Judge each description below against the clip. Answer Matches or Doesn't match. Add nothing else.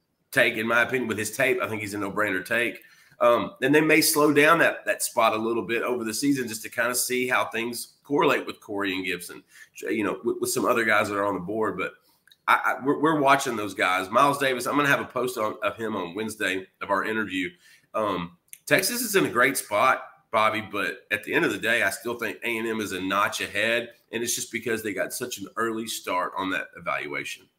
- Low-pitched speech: Matches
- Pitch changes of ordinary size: Matches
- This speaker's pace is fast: Matches